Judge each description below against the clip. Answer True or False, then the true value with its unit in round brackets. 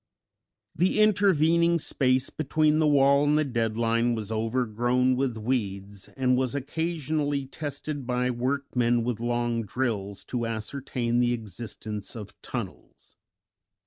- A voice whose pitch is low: True (125 Hz)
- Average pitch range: True (3.7 semitones)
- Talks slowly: True (125 wpm)